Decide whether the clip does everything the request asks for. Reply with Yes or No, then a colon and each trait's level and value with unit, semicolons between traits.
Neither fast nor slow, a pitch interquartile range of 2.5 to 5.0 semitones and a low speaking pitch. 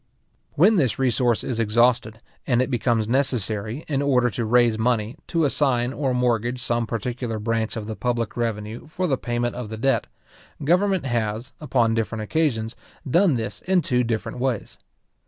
Yes: average, 165 wpm; average, 2.9 semitones; low, 120 Hz